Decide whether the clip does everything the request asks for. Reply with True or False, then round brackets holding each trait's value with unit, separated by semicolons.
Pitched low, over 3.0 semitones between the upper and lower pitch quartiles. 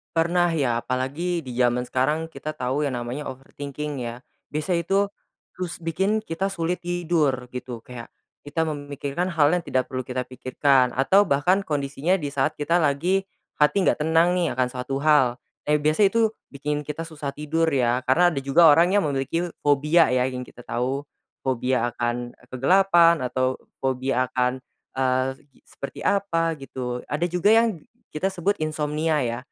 False (145 Hz; 4.7 semitones)